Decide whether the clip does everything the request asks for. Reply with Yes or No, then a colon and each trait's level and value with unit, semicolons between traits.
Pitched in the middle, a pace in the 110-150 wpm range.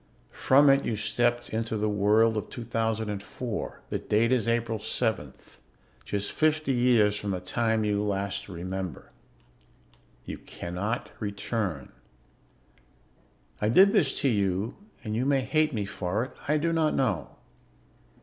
No: low, 110 Hz; average, 140 wpm